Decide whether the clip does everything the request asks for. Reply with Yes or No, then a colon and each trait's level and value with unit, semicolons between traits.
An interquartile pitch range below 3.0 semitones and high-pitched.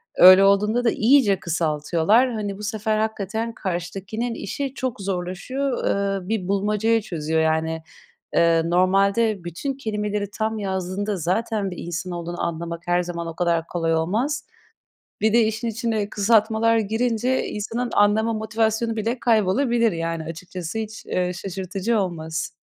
No: average, 4.1 semitones; high, 200 Hz